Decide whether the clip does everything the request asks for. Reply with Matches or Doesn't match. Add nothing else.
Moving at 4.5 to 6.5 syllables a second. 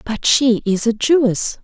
Doesn't match